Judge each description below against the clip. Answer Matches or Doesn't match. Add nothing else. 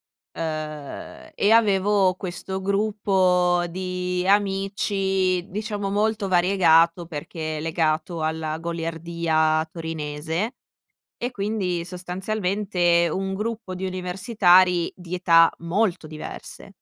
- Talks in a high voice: Doesn't match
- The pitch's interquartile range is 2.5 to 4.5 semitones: Matches